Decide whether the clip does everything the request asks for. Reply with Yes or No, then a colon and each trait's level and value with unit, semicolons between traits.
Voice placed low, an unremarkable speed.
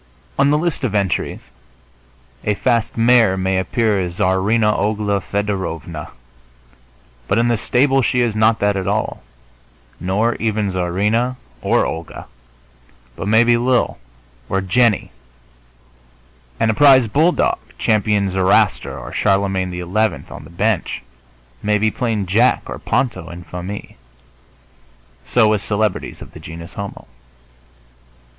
No: low, 105 Hz; slow, 130 wpm